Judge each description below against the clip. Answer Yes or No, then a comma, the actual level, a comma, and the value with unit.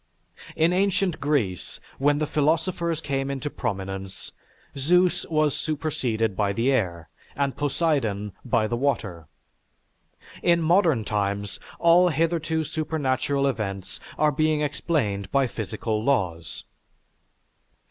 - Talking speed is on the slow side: Yes, slow, 110 wpm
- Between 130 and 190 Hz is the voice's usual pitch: Yes, medium, 140 Hz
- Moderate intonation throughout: No, wide, 7.0 semitones